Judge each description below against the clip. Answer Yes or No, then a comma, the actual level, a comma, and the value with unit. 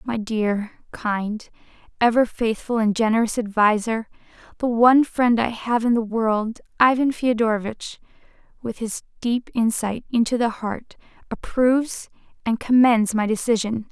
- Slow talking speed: Yes, slow, 130 wpm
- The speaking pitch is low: No, high, 225 Hz